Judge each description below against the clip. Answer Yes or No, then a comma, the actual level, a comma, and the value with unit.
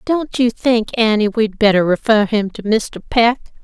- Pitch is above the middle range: Yes, high, 220 Hz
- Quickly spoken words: No, average, 180 wpm